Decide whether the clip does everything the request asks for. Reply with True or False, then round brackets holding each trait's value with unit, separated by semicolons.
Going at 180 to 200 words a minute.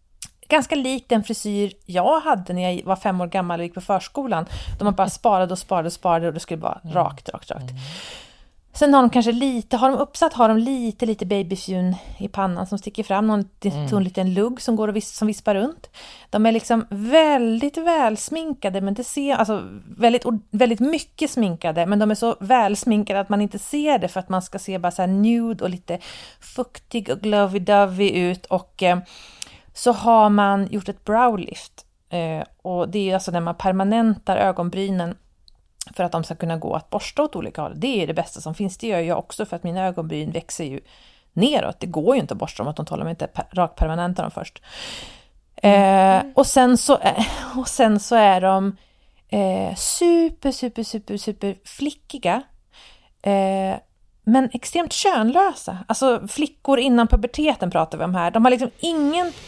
True (190 wpm)